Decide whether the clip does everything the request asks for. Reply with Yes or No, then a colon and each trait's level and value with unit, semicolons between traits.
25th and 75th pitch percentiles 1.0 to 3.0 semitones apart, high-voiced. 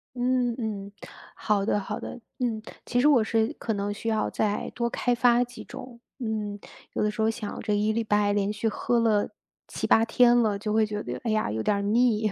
Yes: narrow, 2.4 semitones; high, 220 Hz